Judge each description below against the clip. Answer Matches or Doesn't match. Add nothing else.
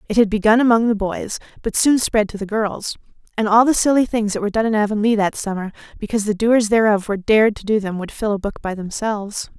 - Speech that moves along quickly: Matches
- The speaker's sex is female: Matches